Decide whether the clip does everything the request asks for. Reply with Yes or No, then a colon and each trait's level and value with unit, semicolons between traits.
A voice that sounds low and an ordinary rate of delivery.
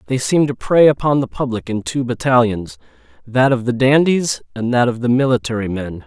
Yes: low, 125 Hz; average, 190 wpm